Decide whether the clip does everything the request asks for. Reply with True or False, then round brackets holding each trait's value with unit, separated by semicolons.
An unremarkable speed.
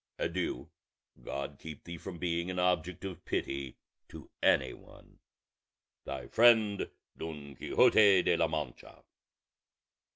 False (120 wpm)